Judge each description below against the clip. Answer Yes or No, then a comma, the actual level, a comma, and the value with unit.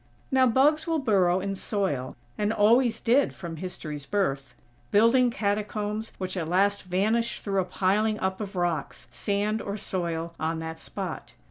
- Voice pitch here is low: No, high, 200 Hz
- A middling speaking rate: Yes, average, 155 wpm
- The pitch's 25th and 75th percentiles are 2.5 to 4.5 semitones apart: Yes, average, 3.9 semitones